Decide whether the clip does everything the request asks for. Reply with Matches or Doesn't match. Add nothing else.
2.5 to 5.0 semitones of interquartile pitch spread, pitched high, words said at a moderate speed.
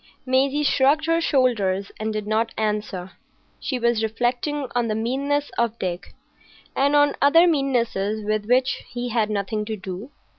Matches